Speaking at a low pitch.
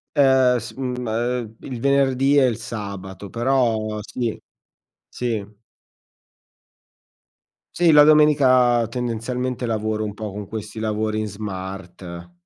Yes: low, 115 Hz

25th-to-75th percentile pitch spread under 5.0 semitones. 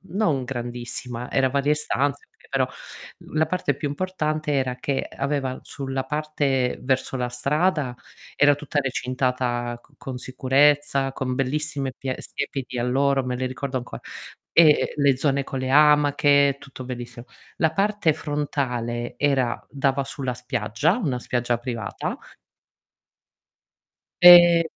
Yes: narrow, 2.6 semitones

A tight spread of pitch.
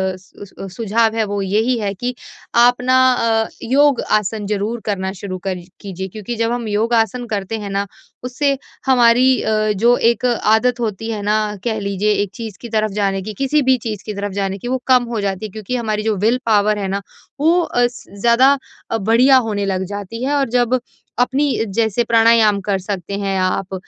No: average, 3.3 semitones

